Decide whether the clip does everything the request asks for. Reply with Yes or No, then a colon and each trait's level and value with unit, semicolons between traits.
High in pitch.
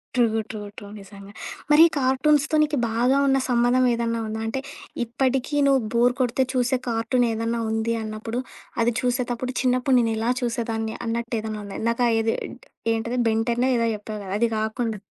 Yes: high, 235 Hz